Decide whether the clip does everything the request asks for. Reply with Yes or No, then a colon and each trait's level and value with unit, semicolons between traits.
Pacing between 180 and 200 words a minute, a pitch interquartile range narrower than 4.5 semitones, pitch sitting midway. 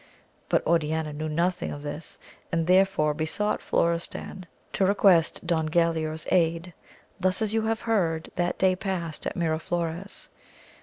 No: average, 140 wpm; average, 2.8 semitones; medium, 170 Hz